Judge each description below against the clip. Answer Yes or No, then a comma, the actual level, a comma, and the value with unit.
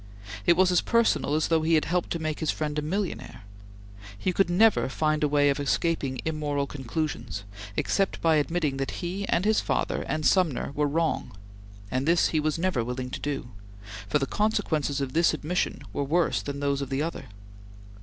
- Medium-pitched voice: Yes, medium, 155 Hz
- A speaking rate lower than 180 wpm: No, average, 195 wpm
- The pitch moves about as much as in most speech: Yes, average, 3.4 semitones